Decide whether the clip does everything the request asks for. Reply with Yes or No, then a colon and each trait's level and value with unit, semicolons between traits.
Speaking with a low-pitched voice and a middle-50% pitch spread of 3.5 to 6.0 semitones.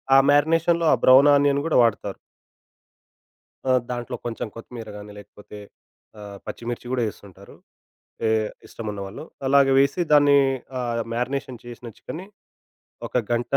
Yes: low, 120 Hz; average, 4.2 semitones